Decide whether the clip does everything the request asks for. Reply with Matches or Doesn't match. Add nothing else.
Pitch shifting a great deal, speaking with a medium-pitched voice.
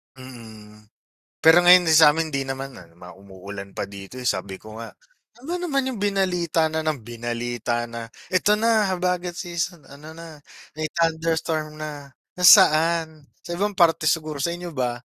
Matches